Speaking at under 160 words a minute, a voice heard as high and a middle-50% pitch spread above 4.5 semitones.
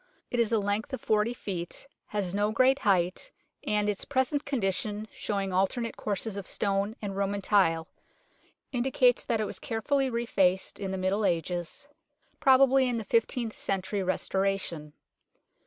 No: average, 150 wpm; high, 205 Hz; average, 3.6 semitones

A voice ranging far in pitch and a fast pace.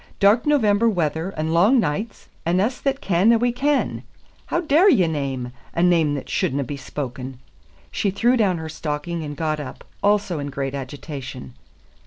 No: wide, 7.0 semitones; average, 175 wpm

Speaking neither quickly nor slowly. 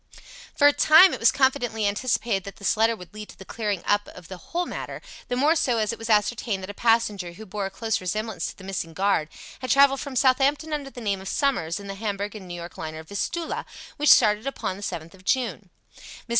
No: fast, 235 wpm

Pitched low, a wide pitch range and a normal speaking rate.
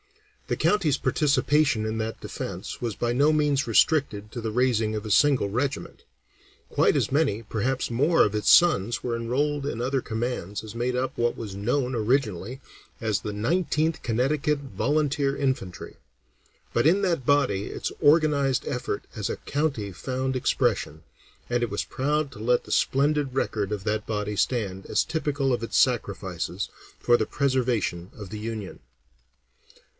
No: low, 125 Hz; average, 4.8 semitones; average, 160 wpm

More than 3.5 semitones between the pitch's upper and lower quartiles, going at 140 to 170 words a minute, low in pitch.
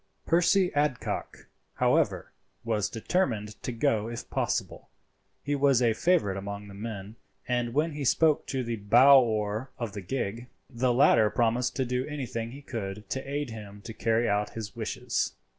Yes: average, 4.0 semitones; average, 165 wpm; low, 120 Hz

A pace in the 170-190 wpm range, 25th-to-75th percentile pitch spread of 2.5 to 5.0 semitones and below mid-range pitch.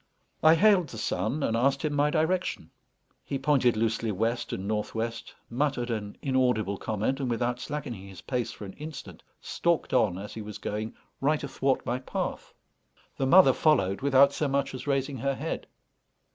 Yes: average, 175 wpm; average, 4.4 semitones; low, 130 Hz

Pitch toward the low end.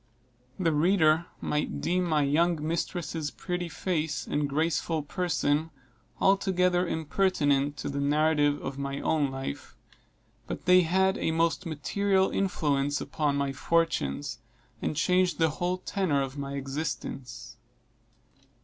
No: medium, 155 Hz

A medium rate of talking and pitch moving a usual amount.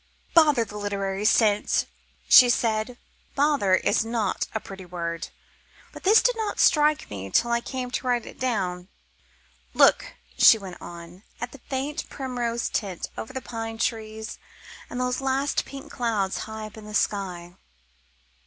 Yes: average, 155 wpm; average, 4.5 semitones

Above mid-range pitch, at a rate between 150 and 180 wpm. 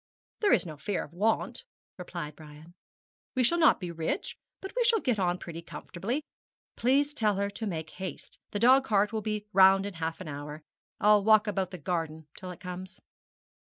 No: high, 195 Hz; average, 190 wpm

